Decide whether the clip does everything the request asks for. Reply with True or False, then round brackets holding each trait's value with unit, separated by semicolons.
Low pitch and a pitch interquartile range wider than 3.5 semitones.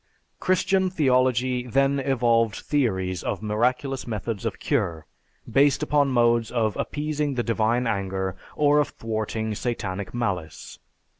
True (120 Hz; 4.2 semitones)